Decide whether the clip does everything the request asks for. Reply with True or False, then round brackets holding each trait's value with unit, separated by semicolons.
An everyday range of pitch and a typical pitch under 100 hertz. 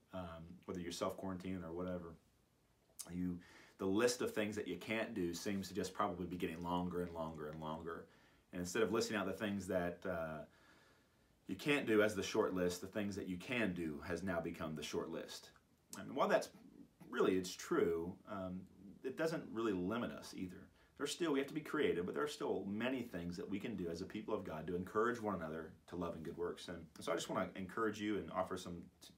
False (2.2 semitones; 90 Hz)